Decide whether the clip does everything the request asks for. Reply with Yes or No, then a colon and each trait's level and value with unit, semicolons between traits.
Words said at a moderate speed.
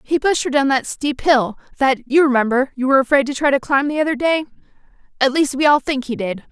No: fast, 250 wpm